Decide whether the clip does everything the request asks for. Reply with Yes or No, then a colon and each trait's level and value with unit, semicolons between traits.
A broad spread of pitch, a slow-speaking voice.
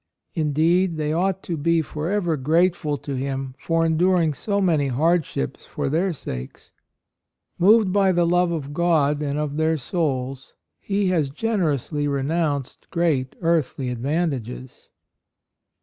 No: average, 3.8 semitones; slow, 130 wpm